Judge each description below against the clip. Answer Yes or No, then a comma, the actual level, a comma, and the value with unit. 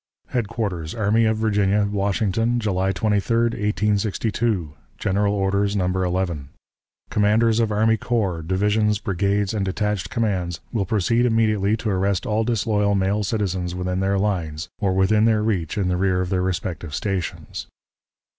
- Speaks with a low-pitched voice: Yes, low, 100 Hz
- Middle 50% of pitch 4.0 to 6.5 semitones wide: No, narrow, 2.5 semitones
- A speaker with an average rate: Yes, average, 145 wpm